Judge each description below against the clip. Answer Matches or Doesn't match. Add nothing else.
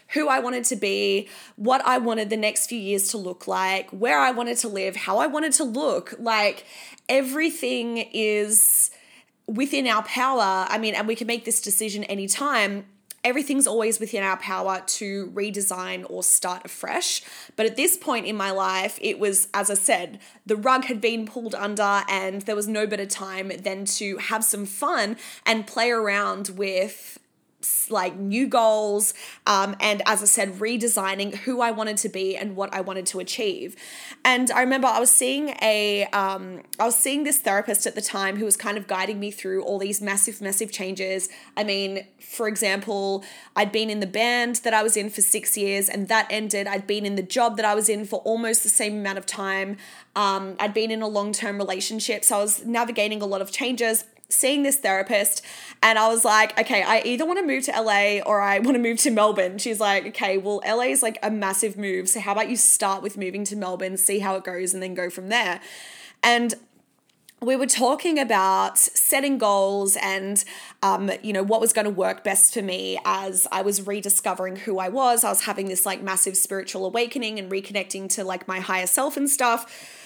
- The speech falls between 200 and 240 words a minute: Matches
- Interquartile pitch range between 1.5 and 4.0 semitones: Matches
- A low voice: Doesn't match